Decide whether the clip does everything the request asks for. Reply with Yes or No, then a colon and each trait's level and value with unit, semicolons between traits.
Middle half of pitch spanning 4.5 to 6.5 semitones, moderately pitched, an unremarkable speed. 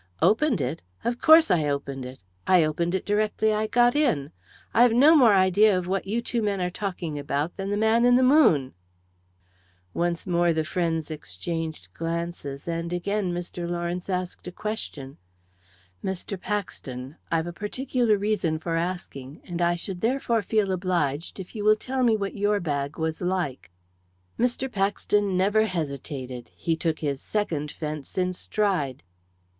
Yes: average, 4.9 semitones; medium, 180 Hz; average, 165 wpm